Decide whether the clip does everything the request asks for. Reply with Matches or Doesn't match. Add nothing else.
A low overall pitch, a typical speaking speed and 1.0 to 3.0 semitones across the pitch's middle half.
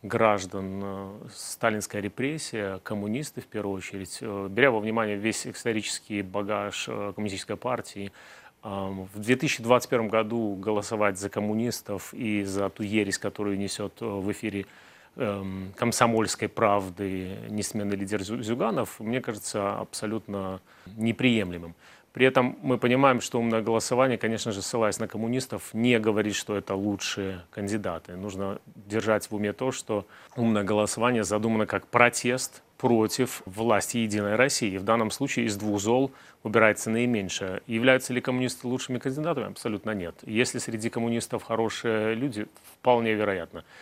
Matches